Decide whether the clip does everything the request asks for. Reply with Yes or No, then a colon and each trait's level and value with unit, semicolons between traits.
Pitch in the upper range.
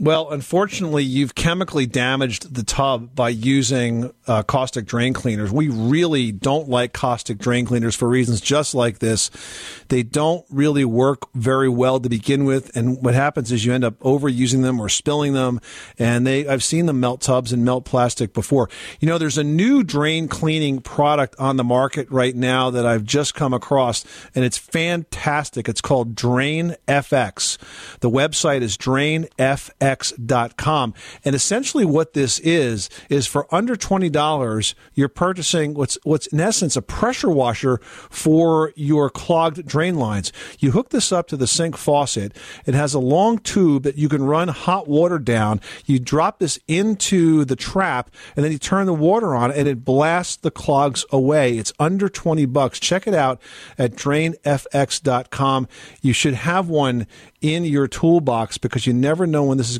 No: medium, 140 Hz